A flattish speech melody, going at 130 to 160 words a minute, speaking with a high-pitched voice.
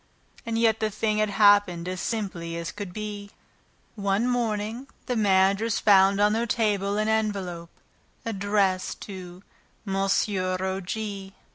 Yes: narrow, 2.1 semitones; slow, 135 wpm; high, 205 Hz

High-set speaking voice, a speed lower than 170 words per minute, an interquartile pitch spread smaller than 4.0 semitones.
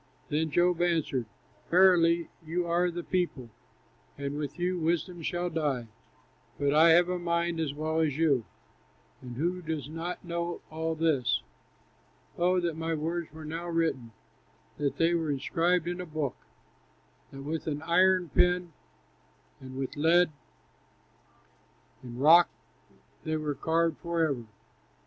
No: medium, 165 Hz; average, 140 wpm; average, 2.7 semitones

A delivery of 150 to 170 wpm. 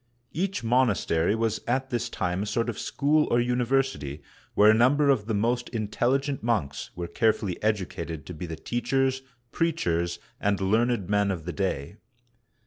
Yes: average, 160 wpm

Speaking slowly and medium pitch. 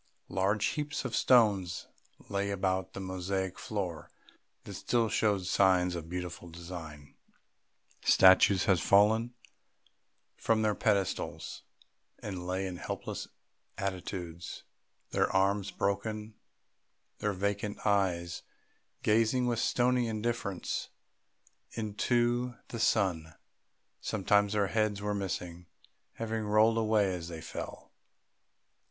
No: slow, 110 wpm; low, 100 Hz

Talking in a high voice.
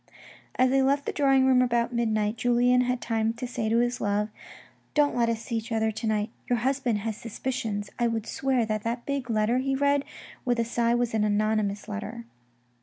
Yes: high, 235 Hz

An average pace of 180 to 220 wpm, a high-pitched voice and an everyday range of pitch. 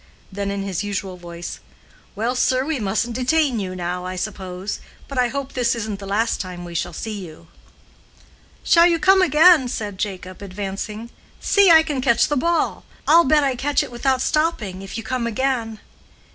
No: average, 185 wpm; high, 225 Hz; wide, 6.0 semitones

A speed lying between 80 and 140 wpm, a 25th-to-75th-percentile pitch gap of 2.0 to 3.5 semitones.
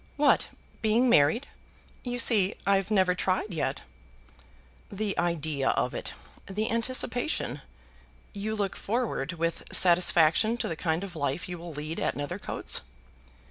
No: slow, 135 wpm; average, 5.0 semitones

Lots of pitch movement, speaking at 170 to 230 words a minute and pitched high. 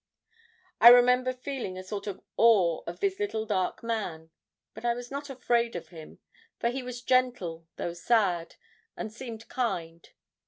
No: wide, 5.7 semitones; average, 160 wpm; high, 230 Hz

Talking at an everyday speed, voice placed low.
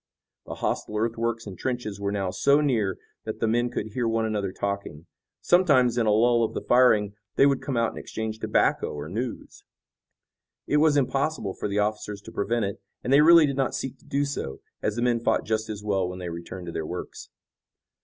No: fast, 215 wpm; low, 110 Hz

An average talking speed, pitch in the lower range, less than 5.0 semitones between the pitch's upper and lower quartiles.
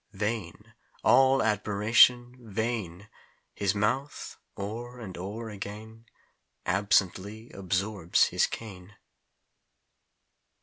No: slow, 80 wpm; low, 105 Hz; average, 2.7 semitones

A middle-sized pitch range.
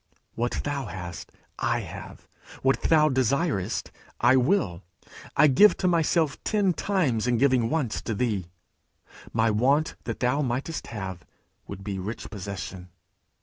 No: wide, 6.5 semitones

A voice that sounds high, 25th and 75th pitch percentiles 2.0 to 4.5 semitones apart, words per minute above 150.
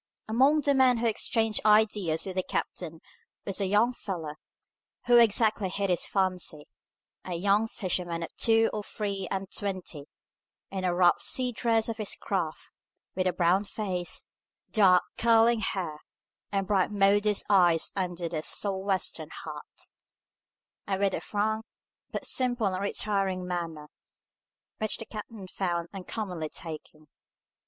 No: high, 195 Hz; average, 3.3 semitones; average, 140 wpm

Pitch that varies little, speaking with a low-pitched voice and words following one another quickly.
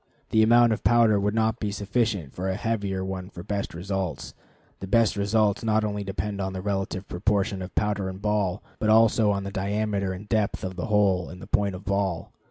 Yes: narrow, 2.0 semitones; low, 100 Hz; fast, 210 wpm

